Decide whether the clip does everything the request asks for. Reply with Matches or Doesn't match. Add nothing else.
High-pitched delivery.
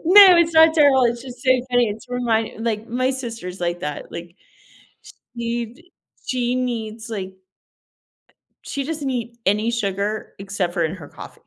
Matches